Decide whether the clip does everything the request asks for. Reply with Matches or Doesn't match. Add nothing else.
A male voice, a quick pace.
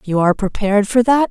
Doesn't match